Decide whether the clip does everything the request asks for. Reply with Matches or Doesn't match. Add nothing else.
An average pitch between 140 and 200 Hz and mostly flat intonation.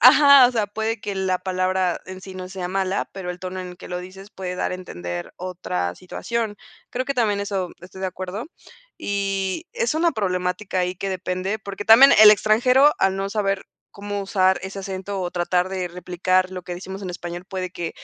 Matches